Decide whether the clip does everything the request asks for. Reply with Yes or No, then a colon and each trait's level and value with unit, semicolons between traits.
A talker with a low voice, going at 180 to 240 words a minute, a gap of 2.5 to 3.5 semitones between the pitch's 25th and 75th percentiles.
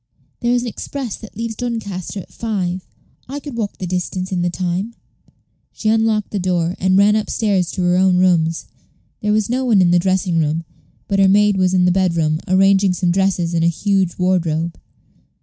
No: high, 190 Hz; average, 200 wpm; average, 3.0 semitones